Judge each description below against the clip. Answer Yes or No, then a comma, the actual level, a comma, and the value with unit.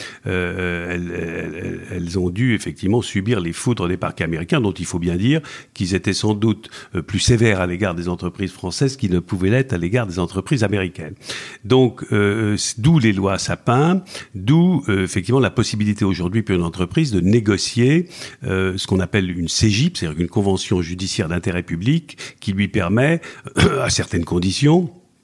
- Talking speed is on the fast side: No, average, 175 wpm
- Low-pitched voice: Yes, low, 100 Hz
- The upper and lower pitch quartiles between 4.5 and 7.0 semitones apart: Yes, average, 5.3 semitones